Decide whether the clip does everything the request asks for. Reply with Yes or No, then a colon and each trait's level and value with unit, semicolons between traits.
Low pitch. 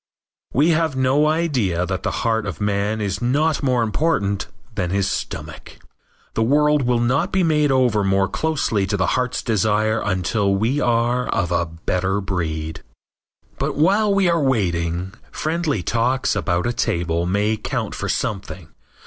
Yes: low, 110 Hz